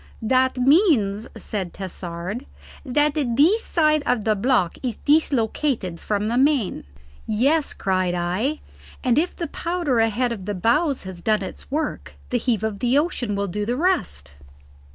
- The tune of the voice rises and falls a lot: Yes, wide, 6.4 semitones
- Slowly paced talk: No, average, 155 wpm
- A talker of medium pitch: No, high, 240 Hz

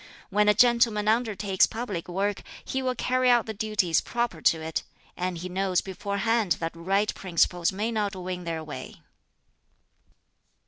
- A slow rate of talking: No, average, 150 wpm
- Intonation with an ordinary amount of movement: Yes, average, 3.8 semitones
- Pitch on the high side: Yes, high, 200 Hz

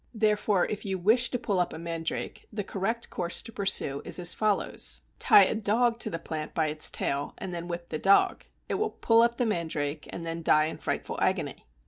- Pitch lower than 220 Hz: Yes, medium, 185 Hz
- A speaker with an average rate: No, fast, 215 wpm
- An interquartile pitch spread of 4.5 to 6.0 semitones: Yes, average, 4.9 semitones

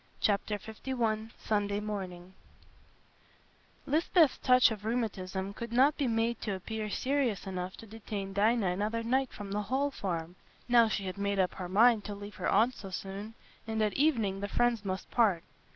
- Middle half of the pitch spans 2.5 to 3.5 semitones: Yes, average, 3.1 semitones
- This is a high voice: Yes, high, 210 Hz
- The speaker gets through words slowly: No, average, 170 wpm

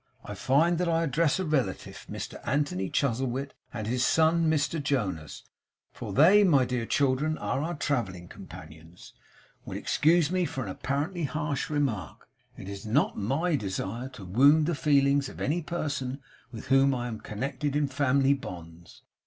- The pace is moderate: Yes, average, 160 wpm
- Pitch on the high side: No, medium, 140 Hz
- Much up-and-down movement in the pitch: No, average, 5.0 semitones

